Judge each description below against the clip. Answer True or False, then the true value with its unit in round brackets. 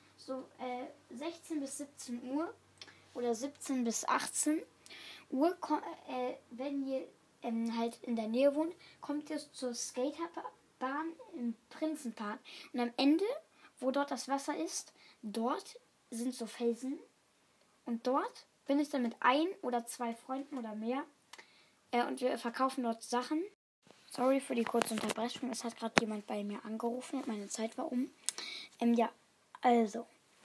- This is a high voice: True (255 Hz)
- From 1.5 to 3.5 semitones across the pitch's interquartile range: False (3.9 semitones)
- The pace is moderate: True (150 wpm)